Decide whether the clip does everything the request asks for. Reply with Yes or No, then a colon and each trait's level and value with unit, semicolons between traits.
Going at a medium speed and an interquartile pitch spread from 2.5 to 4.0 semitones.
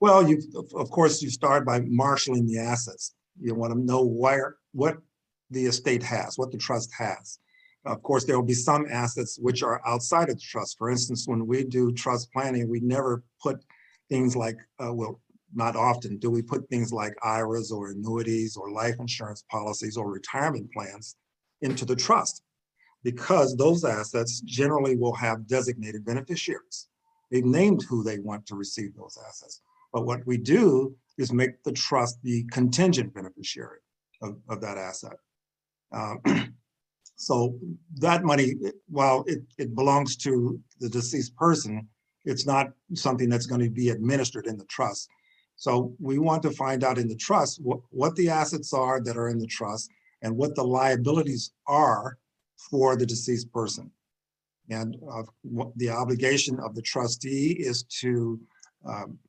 Yes: average, 165 wpm; average, 2.8 semitones